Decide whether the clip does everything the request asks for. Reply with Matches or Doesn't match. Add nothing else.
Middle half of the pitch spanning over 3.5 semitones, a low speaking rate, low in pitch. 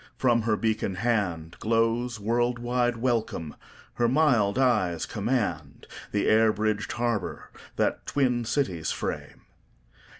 Doesn't match